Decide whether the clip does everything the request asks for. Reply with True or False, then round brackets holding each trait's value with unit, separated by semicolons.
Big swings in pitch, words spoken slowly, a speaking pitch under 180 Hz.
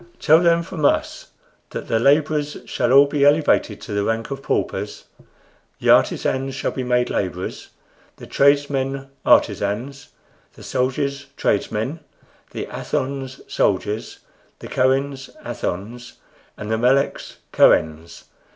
False (3.6 semitones; 125 wpm; 135 Hz)